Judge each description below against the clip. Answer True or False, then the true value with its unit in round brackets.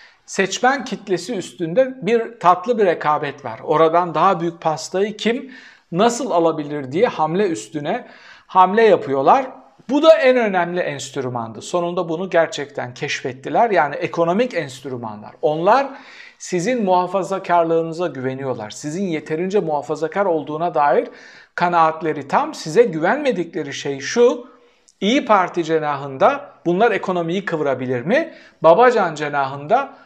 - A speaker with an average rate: True (110 wpm)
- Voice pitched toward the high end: False (170 Hz)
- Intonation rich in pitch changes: True (5.7 semitones)